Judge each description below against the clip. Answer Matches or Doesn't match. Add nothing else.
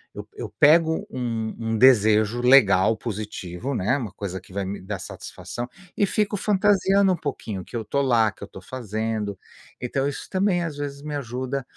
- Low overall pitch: Matches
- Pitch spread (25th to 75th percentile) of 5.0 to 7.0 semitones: Matches